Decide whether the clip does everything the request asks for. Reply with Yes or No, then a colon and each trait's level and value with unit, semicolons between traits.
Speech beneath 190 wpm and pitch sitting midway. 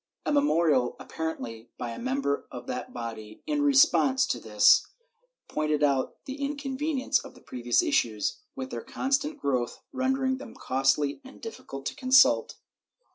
Yes: average, 150 wpm; medium, 165 Hz